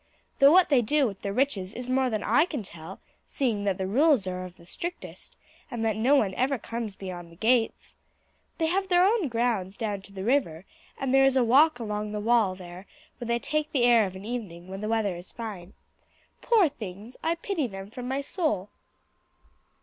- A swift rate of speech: Yes, fast, 210 wpm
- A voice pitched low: No, high, 230 Hz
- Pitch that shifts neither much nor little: No, wide, 5.8 semitones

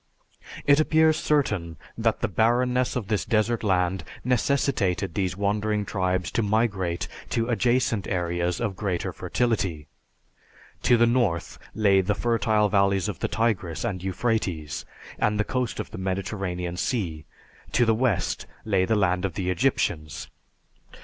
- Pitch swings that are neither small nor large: Yes, average, 4.3 semitones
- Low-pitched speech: Yes, low, 105 Hz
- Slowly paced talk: No, average, 145 wpm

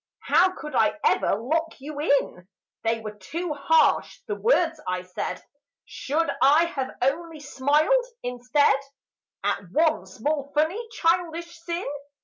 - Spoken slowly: Yes, slow, 130 wpm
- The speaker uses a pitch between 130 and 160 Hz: No, very high, 300 Hz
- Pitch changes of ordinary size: Yes, average, 4.7 semitones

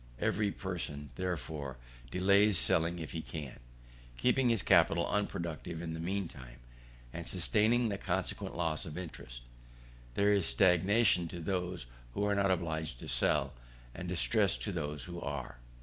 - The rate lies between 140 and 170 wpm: Yes, average, 150 wpm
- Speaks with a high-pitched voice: No, very low, 85 Hz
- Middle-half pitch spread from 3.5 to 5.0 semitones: Yes, average, 3.8 semitones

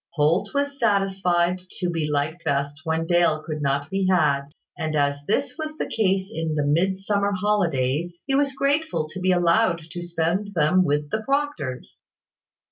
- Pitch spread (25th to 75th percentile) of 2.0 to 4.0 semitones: No, average, 4.8 semitones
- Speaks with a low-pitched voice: No, medium, 175 Hz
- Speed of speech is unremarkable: Yes, average, 165 wpm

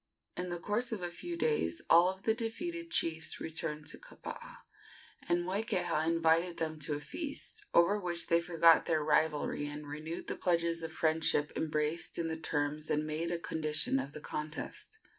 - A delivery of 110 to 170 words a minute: No, average, 180 wpm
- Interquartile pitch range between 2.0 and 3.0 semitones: Yes, narrow, 2.6 semitones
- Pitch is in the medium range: Yes, medium, 165 Hz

